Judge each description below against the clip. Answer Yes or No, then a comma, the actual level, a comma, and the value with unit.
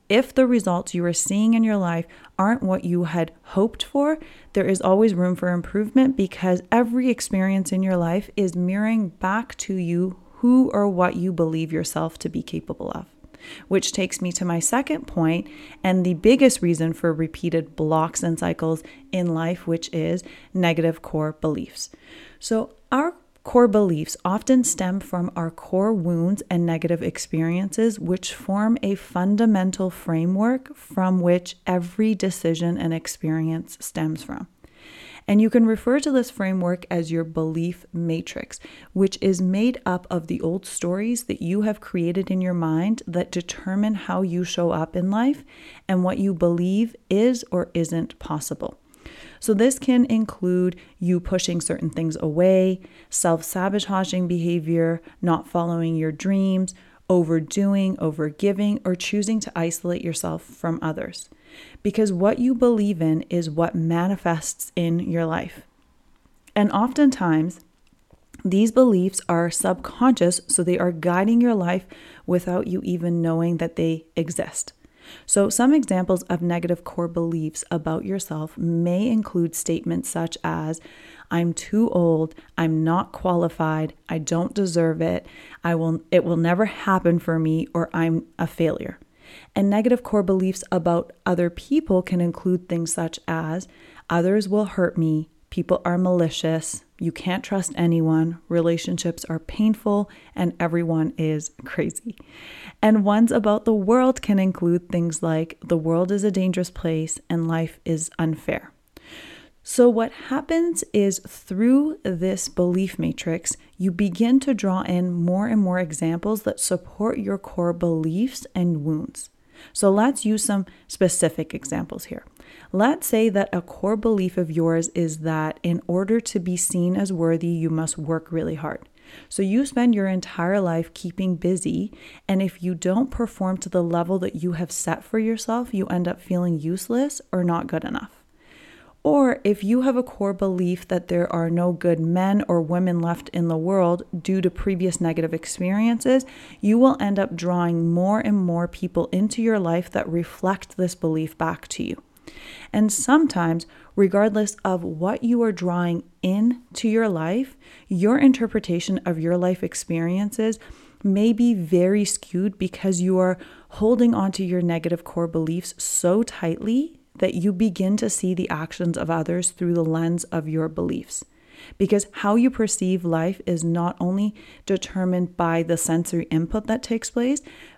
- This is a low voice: No, medium, 180 Hz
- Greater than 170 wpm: No, average, 155 wpm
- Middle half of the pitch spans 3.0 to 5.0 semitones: Yes, average, 3.8 semitones